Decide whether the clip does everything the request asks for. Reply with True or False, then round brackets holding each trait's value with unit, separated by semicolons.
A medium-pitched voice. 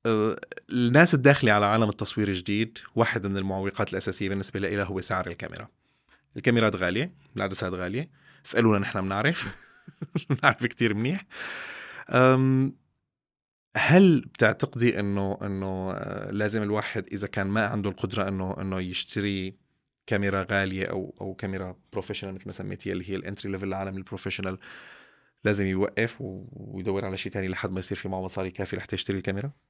False (100 Hz)